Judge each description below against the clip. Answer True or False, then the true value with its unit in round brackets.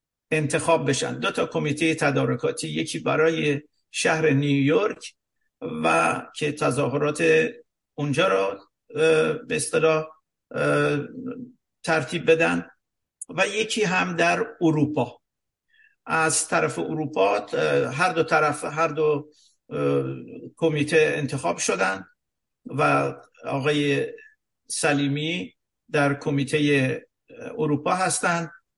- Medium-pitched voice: True (155 Hz)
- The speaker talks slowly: True (85 wpm)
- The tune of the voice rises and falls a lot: False (2.9 semitones)